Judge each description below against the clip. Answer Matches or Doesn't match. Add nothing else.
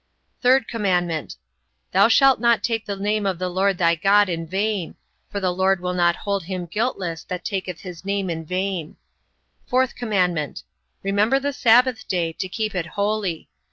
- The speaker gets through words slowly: Doesn't match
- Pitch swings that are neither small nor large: Matches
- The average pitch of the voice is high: Matches